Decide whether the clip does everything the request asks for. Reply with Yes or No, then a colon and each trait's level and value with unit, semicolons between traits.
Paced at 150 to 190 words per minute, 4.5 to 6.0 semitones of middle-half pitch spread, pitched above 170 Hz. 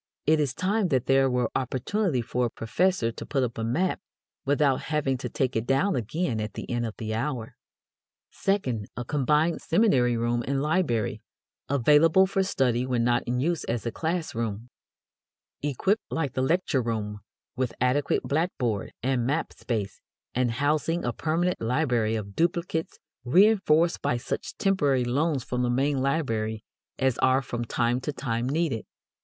No: average, 165 wpm; average, 5.1 semitones; low, 130 Hz